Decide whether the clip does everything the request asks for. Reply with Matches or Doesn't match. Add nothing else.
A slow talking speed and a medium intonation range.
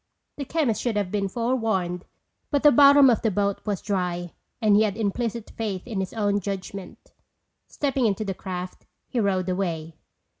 Doesn't match